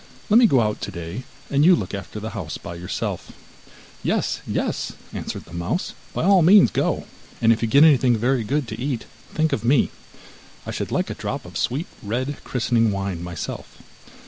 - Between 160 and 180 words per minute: No, average, 190 wpm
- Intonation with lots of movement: Yes, wide, 5.8 semitones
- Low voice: Yes, low, 120 Hz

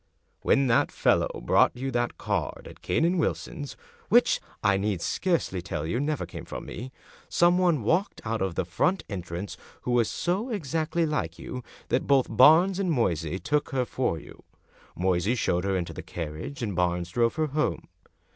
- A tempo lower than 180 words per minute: No, average, 185 wpm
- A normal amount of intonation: No, wide, 9.0 semitones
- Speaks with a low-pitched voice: Yes, low, 120 Hz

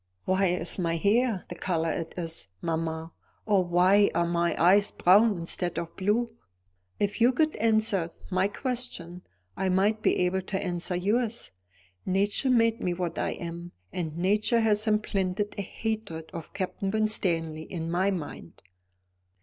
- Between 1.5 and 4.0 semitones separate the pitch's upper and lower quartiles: Yes, average, 3.7 semitones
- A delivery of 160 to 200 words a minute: No, average, 150 wpm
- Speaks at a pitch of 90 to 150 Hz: No, high, 190 Hz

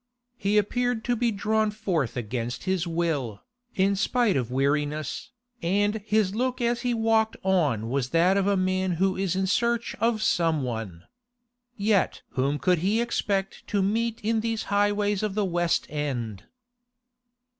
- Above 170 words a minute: No, average, 155 wpm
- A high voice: Yes, high, 195 Hz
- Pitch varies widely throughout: Yes, wide, 6.1 semitones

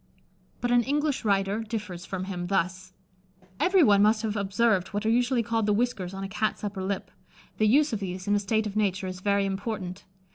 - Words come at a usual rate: No, fast, 210 wpm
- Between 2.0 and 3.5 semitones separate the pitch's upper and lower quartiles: Yes, average, 2.8 semitones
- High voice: Yes, high, 205 Hz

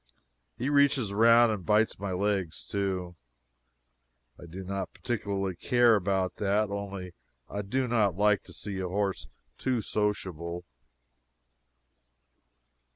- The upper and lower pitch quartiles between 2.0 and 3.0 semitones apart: Yes, narrow, 2.5 semitones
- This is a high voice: No, low, 100 Hz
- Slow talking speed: Yes, slow, 120 wpm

